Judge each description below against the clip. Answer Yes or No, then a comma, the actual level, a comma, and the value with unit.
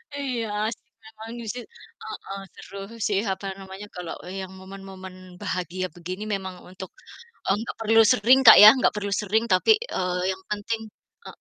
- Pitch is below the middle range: No, high, 195 Hz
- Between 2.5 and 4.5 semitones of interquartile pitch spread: Yes, average, 2.9 semitones